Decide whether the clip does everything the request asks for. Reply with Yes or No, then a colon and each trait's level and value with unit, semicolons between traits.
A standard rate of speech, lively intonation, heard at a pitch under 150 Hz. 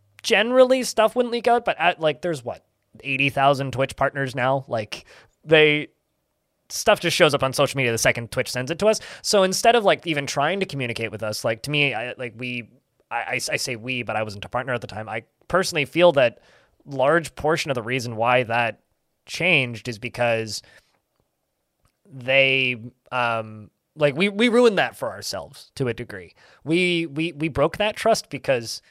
Yes: average, 190 wpm; wide, 5.7 semitones; low, 135 Hz